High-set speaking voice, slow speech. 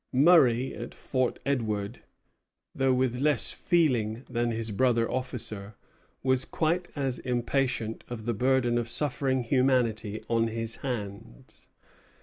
No: low, 120 Hz; slow, 125 wpm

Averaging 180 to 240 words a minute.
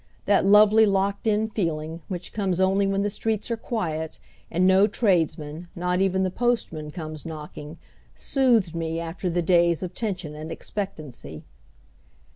No: average, 150 wpm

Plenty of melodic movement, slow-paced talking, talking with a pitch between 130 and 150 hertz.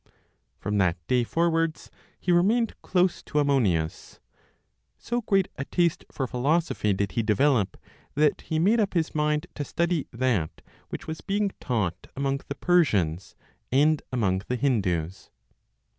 No: wide, 8.3 semitones; average, 145 wpm; medium, 140 Hz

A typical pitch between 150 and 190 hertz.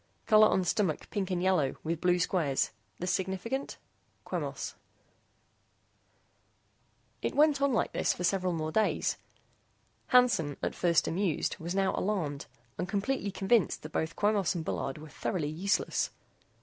Yes: medium, 185 Hz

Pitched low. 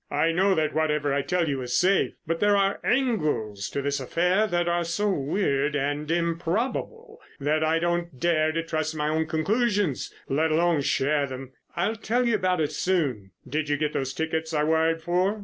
No: medium, 160 Hz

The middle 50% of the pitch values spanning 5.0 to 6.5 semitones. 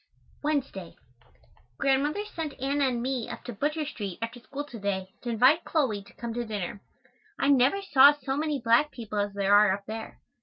Yes: wide, 5.5 semitones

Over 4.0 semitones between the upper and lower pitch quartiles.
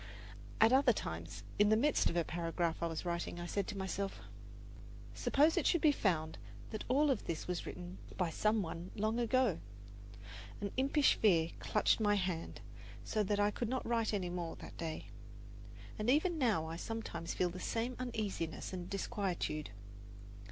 Yes: average, 5.1 semitones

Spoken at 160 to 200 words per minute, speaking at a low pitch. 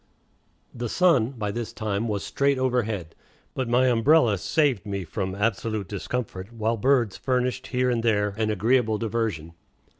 No: average, 150 wpm; low, 115 Hz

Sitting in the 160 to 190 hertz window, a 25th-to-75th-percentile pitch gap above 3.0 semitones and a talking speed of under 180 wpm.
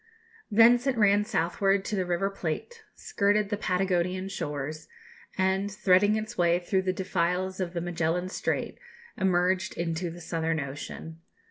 No: medium, 185 Hz; average, 2.7 semitones; average, 145 wpm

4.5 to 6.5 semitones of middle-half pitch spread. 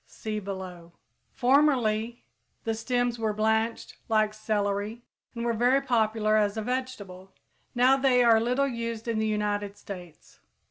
No: narrow, 2.6 semitones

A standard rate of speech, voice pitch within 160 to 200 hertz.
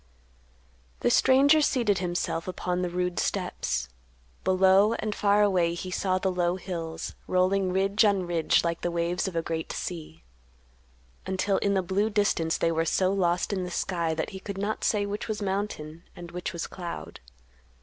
Yes: average, 175 wpm; medium, 185 Hz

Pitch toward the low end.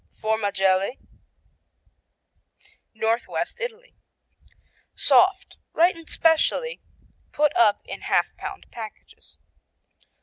No: very high, 295 Hz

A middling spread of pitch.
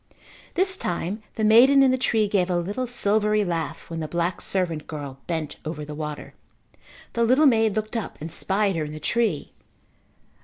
No: wide, 5.7 semitones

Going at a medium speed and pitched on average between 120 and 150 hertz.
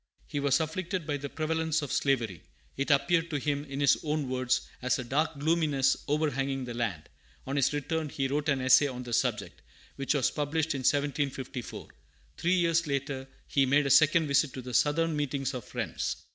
Yes: average, 190 wpm; medium, 140 Hz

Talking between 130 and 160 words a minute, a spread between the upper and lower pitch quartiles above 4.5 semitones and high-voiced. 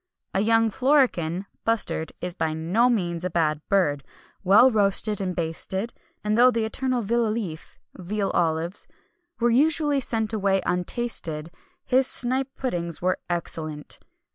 Yes: slow, 135 wpm; wide, 5.6 semitones; high, 200 Hz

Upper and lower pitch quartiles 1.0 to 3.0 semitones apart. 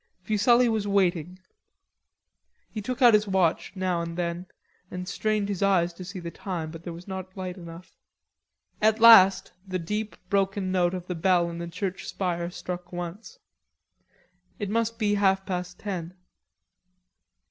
Yes: average, 2.7 semitones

